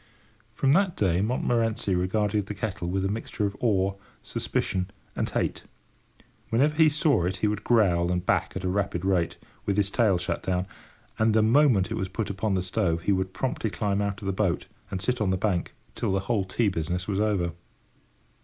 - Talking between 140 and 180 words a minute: No, average, 200 wpm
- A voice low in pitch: Yes, low, 100 Hz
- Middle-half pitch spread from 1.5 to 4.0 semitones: Yes, average, 2.9 semitones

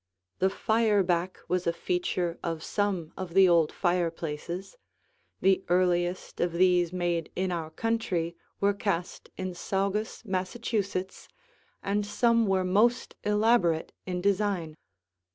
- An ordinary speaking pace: No, slow, 120 wpm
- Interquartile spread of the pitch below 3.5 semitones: Yes, average, 2.7 semitones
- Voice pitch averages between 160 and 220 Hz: Yes, medium, 185 Hz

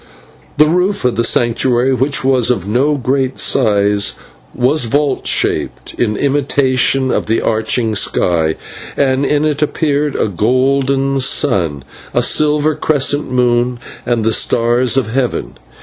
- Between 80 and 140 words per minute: Yes, slow, 135 wpm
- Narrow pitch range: No, average, 3.5 semitones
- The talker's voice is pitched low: Yes, low, 130 Hz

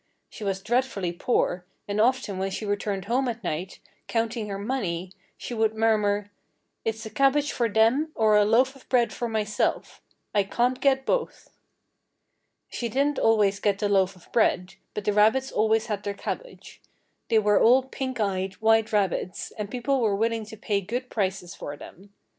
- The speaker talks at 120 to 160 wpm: No, average, 175 wpm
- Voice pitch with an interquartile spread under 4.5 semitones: Yes, average, 3.2 semitones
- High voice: Yes, high, 220 Hz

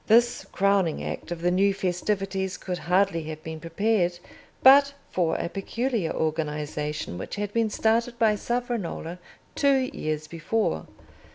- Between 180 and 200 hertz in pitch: Yes, high, 190 Hz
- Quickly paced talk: No, slow, 135 wpm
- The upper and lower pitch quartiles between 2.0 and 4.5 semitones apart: No, average, 5.3 semitones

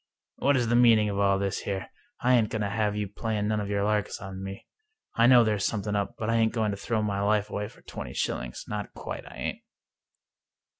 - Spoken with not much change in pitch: Yes, narrow, 1.9 semitones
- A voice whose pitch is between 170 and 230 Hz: No, low, 105 Hz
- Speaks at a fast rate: Yes, fast, 235 wpm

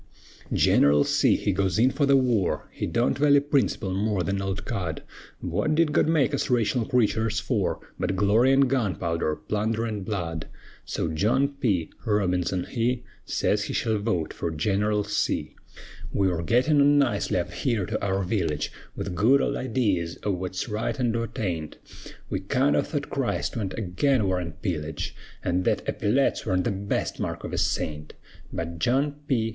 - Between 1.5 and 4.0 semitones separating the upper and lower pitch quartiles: No, wide, 5.6 semitones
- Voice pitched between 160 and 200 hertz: No, low, 105 Hz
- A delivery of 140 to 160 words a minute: No, average, 175 wpm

